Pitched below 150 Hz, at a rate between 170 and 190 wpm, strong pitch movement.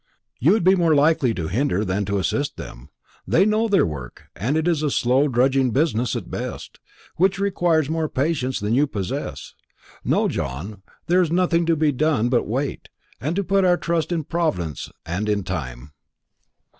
Yes: medium, 140 Hz; average, 180 wpm; wide, 8.2 semitones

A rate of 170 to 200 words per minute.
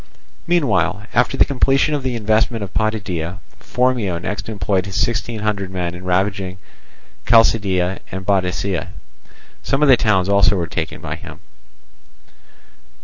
No: average, 140 wpm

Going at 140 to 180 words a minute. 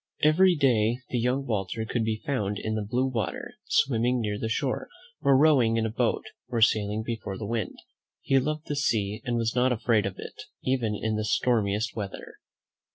No: average, 190 wpm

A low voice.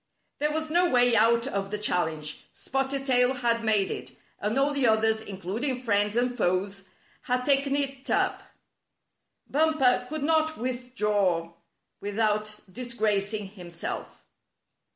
No: high, 230 Hz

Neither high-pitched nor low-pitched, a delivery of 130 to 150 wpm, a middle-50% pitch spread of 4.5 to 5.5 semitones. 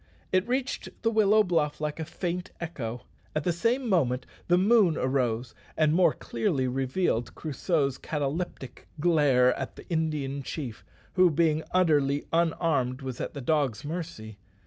Yes: medium, 155 Hz; average, 145 wpm; average, 4.9 semitones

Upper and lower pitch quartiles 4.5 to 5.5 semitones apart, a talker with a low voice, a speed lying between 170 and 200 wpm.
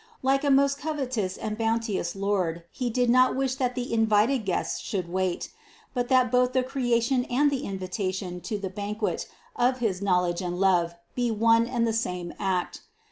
No: average, 5.0 semitones; high, 225 Hz; average, 185 wpm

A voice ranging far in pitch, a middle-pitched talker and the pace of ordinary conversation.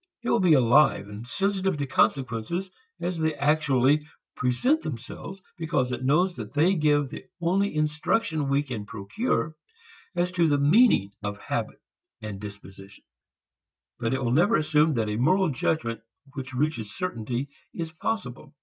Yes: wide, 6.0 semitones; medium, 145 Hz; average, 150 wpm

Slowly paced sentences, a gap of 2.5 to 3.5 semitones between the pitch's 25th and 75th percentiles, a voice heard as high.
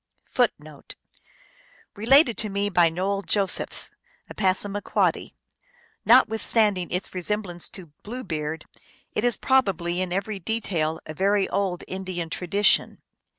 Yes: slow, 125 wpm; average, 3.1 semitones; high, 195 Hz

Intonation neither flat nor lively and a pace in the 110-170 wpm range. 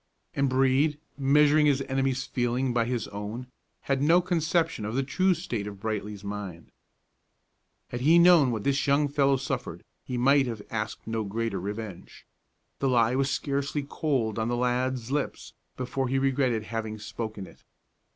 Yes: average, 3.9 semitones; average, 160 wpm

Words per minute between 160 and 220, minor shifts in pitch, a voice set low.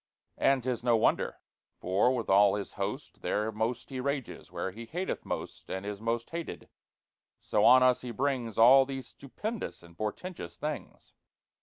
No: average, 165 wpm; average, 4.5 semitones; low, 120 Hz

